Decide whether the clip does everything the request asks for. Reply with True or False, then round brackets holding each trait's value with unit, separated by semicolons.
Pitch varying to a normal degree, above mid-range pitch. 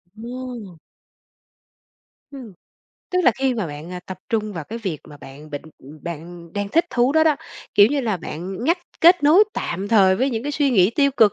False (7.2 semitones; 215 Hz)